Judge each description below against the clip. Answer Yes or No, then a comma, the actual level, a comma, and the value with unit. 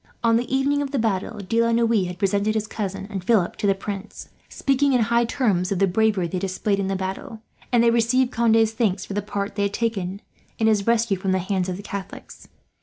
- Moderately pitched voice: No, high, 210 Hz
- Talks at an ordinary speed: No, fast, 240 wpm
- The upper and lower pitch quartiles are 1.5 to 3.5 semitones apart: Yes, average, 3.1 semitones